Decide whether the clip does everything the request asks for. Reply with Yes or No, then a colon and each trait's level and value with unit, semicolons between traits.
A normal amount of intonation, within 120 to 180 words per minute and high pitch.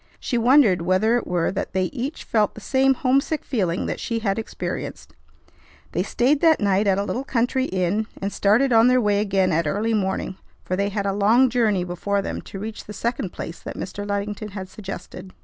No: average, 3.8 semitones; fast, 205 wpm; high, 205 Hz